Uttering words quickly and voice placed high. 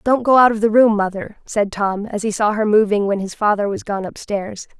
Yes: fast, 250 wpm; high, 210 Hz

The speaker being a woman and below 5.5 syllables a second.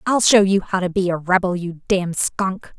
Yes: female; 4.9 syllables/s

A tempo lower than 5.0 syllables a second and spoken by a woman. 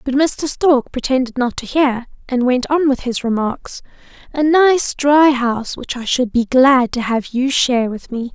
Yes: 4.4 syllables/s; female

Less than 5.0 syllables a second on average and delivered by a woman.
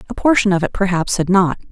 No: 6.4 syllables/s; female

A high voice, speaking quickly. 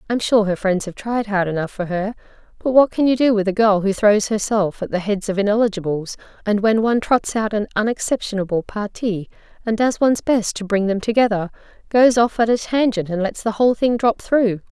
Yes: high, 210 Hz; fast, 220 wpm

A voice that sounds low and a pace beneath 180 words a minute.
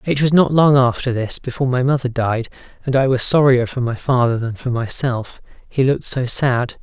No: low, 125 Hz; average, 200 wpm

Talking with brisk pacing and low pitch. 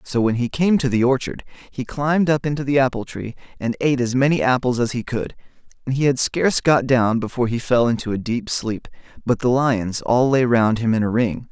Yes: fast, 235 wpm; low, 125 Hz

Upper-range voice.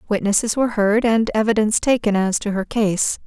Yes: high, 215 Hz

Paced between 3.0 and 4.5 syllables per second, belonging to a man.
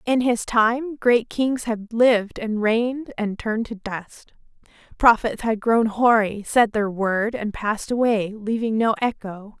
No: 4.0 syllables/s; female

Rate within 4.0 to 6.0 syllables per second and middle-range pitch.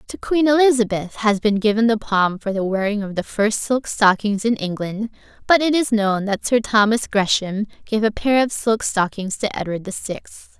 No: 4.7 syllables/s; high, 215 Hz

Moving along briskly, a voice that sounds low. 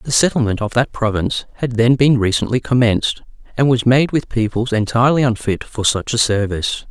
No: average, 180 wpm; low, 120 Hz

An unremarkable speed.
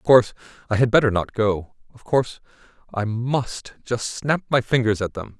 Yes: average, 190 wpm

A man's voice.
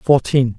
Yes: male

